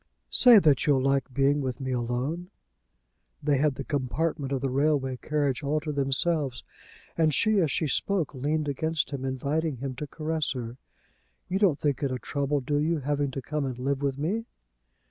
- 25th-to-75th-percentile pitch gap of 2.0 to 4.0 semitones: Yes, narrow, 2.6 semitones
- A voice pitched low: No, medium, 145 Hz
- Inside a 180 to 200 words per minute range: Yes, average, 185 wpm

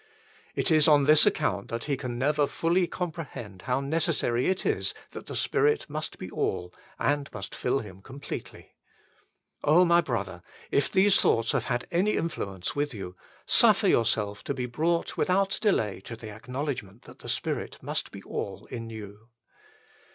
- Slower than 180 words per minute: Yes, average, 165 wpm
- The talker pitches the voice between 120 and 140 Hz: Yes, low, 135 Hz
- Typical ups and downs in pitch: No, wide, 6.6 semitones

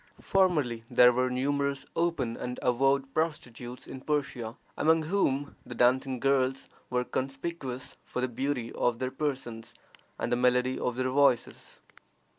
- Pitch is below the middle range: Yes, low, 130 Hz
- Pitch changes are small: Yes, narrow, 2.3 semitones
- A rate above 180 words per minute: No, average, 140 wpm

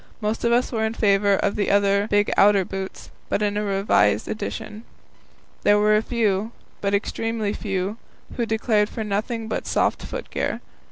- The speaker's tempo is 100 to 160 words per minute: No, average, 170 wpm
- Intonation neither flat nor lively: No, narrow, 1.7 semitones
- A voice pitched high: Yes, high, 210 Hz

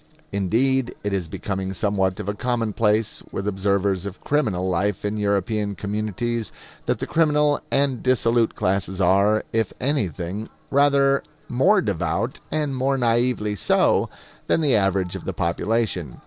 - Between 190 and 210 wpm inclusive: No, average, 140 wpm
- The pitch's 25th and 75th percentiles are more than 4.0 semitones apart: Yes, average, 4.6 semitones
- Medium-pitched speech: No, low, 105 Hz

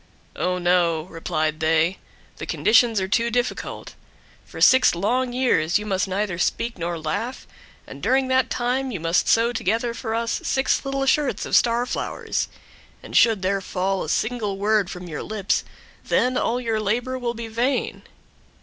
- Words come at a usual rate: Yes, average, 165 wpm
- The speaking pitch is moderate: No, high, 220 Hz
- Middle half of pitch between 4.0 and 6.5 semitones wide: Yes, average, 5.1 semitones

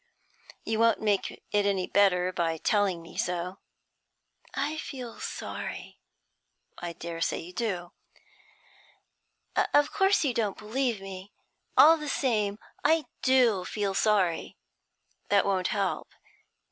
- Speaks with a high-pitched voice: Yes, high, 205 Hz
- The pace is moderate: No, slow, 120 wpm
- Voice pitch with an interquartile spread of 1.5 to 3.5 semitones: No, average, 5.0 semitones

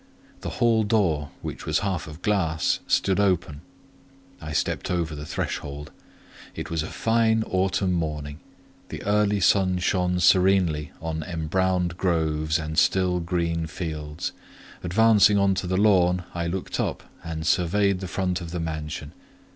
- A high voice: No, very low, 90 Hz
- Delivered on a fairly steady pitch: No, average, 3.3 semitones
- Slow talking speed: No, average, 145 wpm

